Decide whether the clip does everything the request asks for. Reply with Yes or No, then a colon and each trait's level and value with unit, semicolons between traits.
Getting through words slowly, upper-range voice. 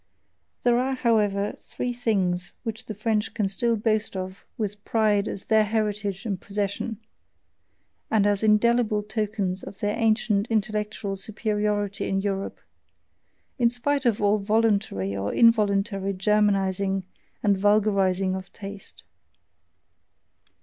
Yes: slow, 120 wpm; high, 210 Hz